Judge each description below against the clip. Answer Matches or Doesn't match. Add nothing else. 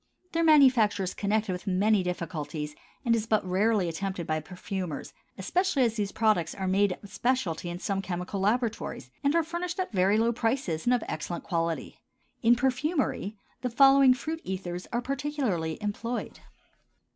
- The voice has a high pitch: Matches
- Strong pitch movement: Matches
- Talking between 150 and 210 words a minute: Matches